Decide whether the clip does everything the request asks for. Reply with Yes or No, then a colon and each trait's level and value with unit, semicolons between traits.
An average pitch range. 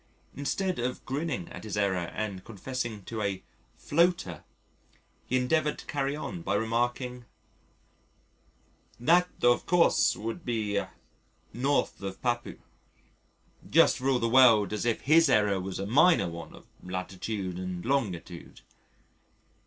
No: wide, 5.7 semitones